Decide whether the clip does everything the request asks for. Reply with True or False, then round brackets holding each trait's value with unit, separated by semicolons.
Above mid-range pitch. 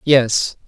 False (125 Hz)